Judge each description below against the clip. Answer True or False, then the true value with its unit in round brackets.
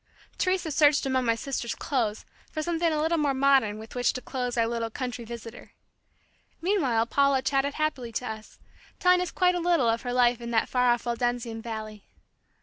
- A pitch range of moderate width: True (4.2 semitones)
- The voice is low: False (250 Hz)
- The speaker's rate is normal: True (190 wpm)